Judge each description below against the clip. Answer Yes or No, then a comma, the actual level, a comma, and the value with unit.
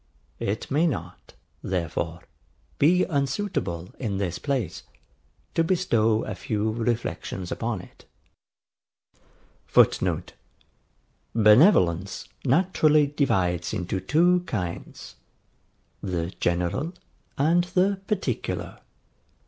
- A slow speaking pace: Yes, slow, 85 wpm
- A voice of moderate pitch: No, low, 115 Hz